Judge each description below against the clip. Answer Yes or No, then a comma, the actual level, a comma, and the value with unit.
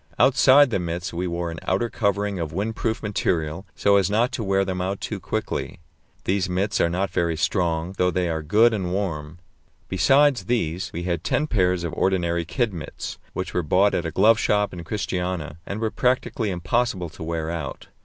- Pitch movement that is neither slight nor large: Yes, average, 3.6 semitones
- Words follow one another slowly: No, average, 195 wpm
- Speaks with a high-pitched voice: No, very low, 95 Hz